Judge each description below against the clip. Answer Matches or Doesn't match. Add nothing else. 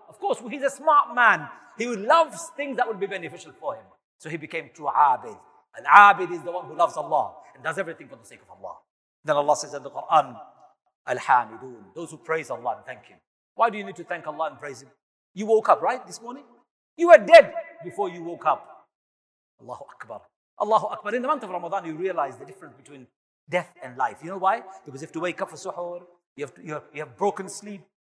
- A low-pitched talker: Doesn't match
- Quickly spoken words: Matches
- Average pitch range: Doesn't match